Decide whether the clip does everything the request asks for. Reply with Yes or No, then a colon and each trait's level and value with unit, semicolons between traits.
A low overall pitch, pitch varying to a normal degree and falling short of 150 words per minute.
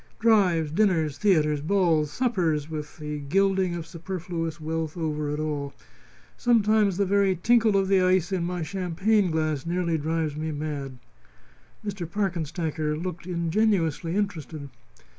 No: medium, 170 Hz; average, 3.8 semitones; slow, 135 wpm